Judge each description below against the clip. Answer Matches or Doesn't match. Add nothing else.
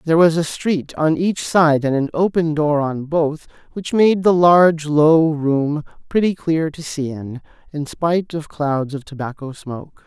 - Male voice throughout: Matches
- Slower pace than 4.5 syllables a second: Matches